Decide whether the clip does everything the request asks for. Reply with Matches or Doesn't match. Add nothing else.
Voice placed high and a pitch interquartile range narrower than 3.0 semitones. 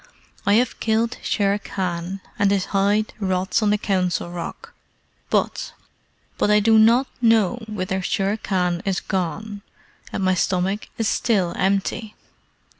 Matches